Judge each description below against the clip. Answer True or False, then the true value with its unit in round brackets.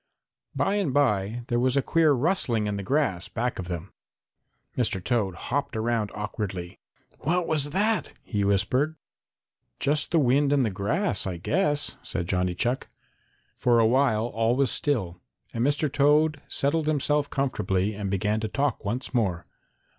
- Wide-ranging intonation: True (6.1 semitones)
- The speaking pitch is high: False (120 Hz)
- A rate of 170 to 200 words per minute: False (160 wpm)